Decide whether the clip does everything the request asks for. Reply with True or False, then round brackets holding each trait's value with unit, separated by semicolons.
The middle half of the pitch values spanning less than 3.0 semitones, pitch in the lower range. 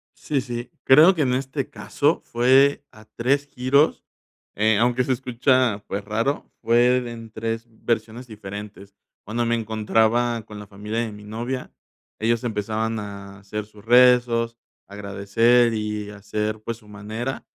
True (2.6 semitones; 115 Hz)